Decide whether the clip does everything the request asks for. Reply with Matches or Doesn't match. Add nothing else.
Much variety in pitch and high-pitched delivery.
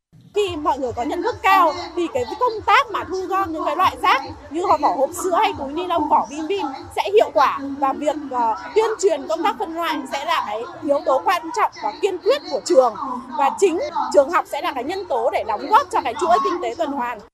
Matches